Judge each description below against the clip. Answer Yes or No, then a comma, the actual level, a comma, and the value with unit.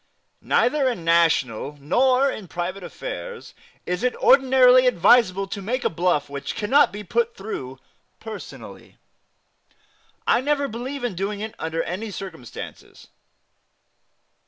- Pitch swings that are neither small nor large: No, wide, 6.6 semitones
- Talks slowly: Yes, slow, 125 wpm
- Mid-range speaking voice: No, high, 210 Hz